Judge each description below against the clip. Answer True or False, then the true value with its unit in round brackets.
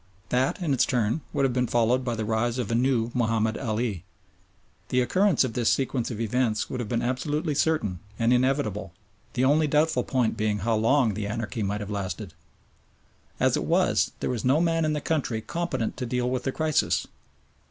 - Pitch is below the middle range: True (125 Hz)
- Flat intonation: False (3.5 semitones)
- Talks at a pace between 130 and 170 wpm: False (195 wpm)